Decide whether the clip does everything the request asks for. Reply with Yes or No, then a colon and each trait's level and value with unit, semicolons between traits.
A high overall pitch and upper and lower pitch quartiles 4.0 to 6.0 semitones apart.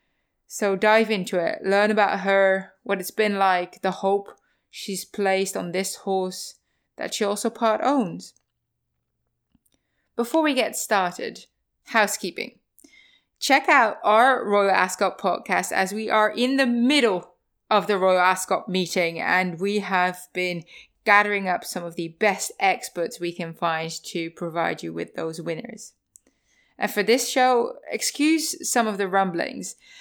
No: high, 200 Hz; average, 3.6 semitones